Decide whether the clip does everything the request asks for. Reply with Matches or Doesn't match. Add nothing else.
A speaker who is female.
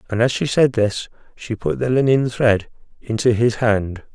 Doesn't match